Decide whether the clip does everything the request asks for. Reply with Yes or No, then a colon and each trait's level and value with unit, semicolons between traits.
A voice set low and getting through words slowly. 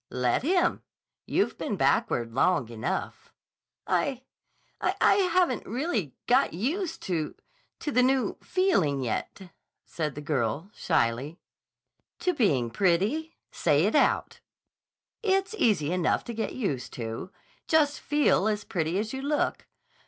No: high, 200 Hz; slow, 125 wpm